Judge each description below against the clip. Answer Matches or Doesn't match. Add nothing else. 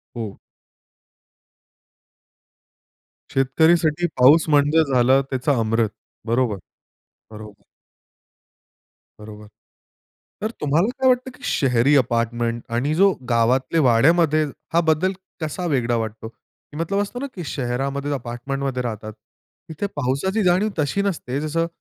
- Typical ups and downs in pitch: Doesn't match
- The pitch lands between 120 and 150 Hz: Matches